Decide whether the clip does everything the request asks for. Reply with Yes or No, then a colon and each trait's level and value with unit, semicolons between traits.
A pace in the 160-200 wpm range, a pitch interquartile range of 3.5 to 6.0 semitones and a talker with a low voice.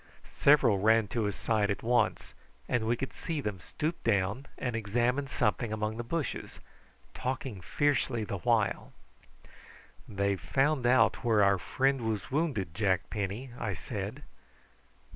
No: average, 145 wpm; average, 4.2 semitones; low, 115 Hz